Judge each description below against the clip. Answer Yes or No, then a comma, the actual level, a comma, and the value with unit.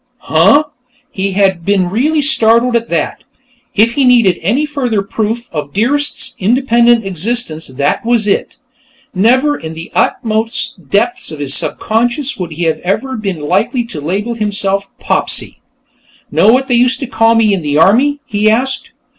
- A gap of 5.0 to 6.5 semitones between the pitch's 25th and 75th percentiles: No, average, 4.3 semitones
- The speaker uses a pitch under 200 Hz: No, high, 220 Hz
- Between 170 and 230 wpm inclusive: No, average, 155 wpm